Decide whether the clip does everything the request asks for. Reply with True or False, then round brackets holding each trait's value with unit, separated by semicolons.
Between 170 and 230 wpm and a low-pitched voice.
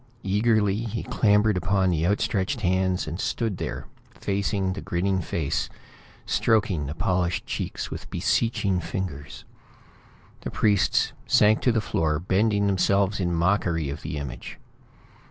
False (135 wpm; 95 Hz)